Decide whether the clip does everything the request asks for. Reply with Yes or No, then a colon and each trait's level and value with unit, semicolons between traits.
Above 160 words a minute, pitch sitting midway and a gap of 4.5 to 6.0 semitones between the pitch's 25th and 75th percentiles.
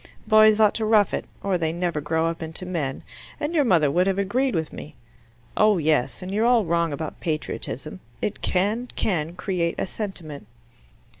Yes: average, 180 wpm; medium, 180 Hz; average, 4.8 semitones